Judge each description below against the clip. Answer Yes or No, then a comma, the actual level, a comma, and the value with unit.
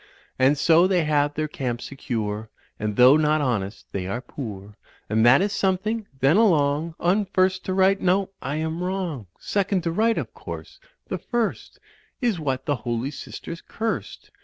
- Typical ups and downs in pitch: No, wide, 6.7 semitones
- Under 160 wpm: No, average, 180 wpm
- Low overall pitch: No, medium, 155 Hz